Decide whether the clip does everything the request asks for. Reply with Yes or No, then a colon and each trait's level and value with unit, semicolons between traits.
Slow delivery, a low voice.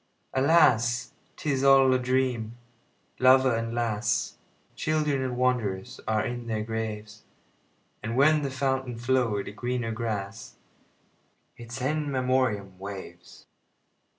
Yes: slow, 100 wpm; low, 120 Hz